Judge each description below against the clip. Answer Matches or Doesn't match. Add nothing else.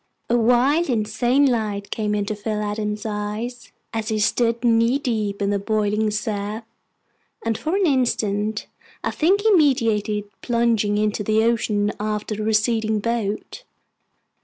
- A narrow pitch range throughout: Matches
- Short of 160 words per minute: Matches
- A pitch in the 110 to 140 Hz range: Doesn't match